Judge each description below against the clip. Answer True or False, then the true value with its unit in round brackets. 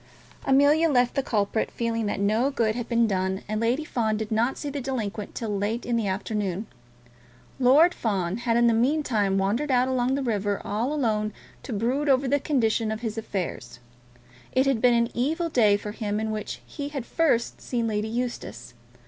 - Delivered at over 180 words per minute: True (190 wpm)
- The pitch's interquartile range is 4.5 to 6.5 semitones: False (3.5 semitones)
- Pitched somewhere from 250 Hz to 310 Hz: False (230 Hz)